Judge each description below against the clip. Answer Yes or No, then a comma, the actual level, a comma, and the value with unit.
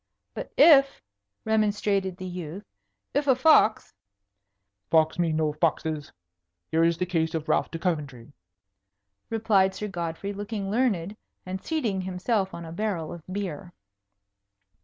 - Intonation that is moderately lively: Yes, average, 4.3 semitones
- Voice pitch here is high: No, medium, 180 Hz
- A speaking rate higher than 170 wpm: No, average, 140 wpm